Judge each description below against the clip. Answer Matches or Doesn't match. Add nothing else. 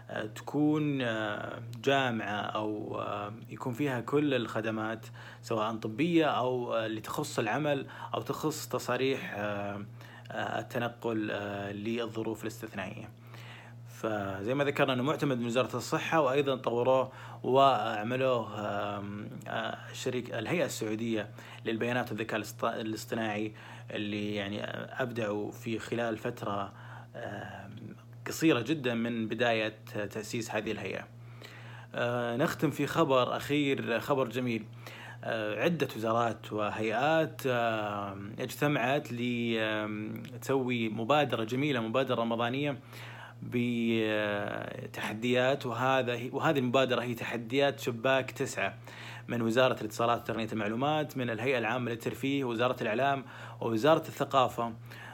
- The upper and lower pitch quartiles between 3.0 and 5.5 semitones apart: Doesn't match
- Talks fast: Doesn't match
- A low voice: Matches